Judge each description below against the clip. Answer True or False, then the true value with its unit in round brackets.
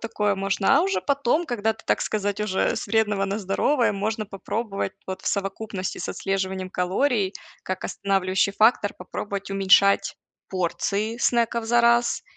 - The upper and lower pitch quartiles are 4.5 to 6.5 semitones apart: False (2.5 semitones)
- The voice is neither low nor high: False (200 Hz)